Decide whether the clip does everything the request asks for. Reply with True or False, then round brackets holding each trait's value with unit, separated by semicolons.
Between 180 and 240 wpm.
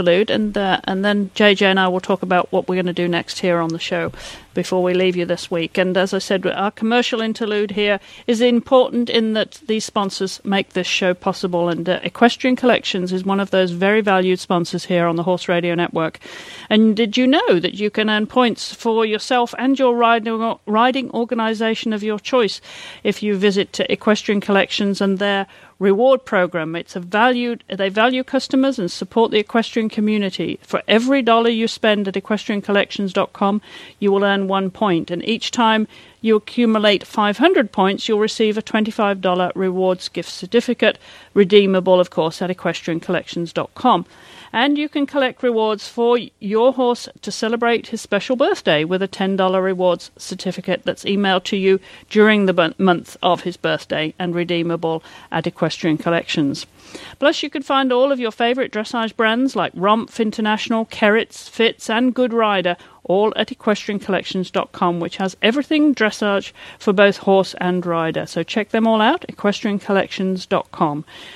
False (170 wpm)